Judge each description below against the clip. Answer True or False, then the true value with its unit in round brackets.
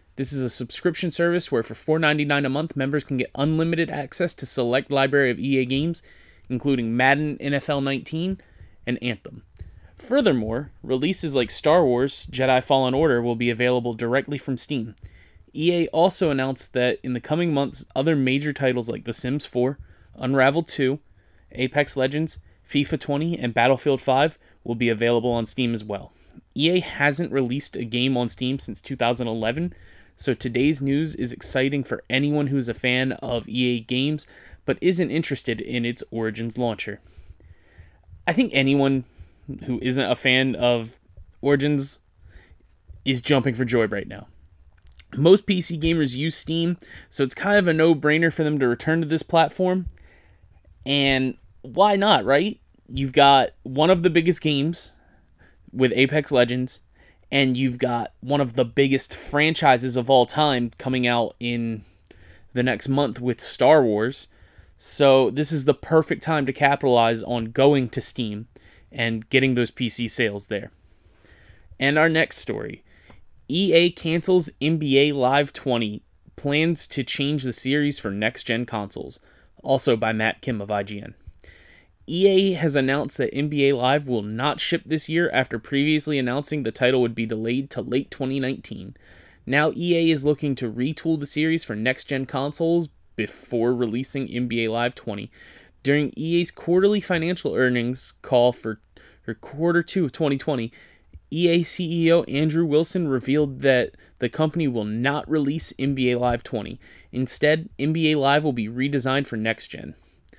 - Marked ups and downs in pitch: False (4.2 semitones)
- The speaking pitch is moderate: False (130 Hz)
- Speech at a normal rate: True (155 wpm)